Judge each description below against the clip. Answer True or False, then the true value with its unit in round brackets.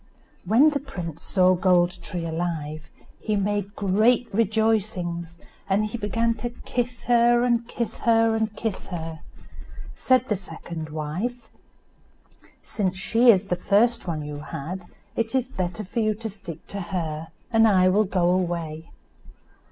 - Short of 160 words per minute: True (150 wpm)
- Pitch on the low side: False (200 Hz)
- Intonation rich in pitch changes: False (4.7 semitones)